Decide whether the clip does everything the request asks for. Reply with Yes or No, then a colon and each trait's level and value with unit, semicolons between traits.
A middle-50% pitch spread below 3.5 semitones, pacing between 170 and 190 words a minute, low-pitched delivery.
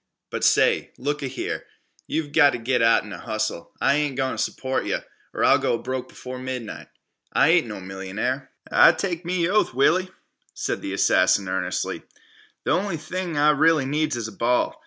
No: wide, 5.5 semitones; average, 180 wpm; low, 130 Hz